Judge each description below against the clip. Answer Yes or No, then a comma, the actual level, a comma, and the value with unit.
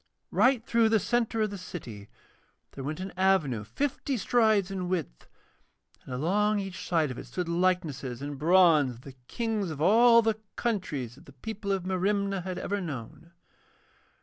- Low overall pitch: No, medium, 185 Hz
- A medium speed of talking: Yes, average, 170 wpm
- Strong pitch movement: Yes, wide, 6.3 semitones